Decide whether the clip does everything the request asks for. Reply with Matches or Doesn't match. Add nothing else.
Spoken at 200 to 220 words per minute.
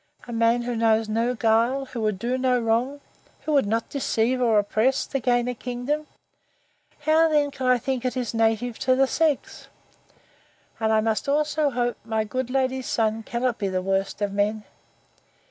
Doesn't match